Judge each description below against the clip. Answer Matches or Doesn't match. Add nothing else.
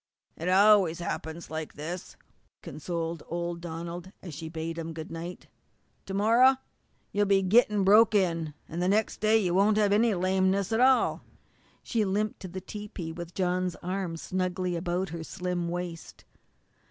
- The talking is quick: Doesn't match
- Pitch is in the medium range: Matches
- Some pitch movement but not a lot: Matches